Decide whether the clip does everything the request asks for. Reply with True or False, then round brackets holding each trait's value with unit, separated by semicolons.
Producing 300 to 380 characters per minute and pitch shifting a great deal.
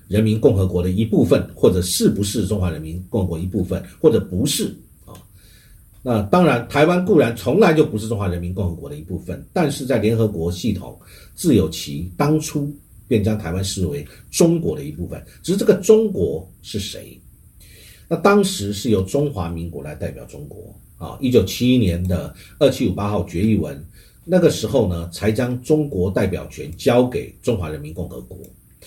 False (285 characters per minute; 7.6 semitones)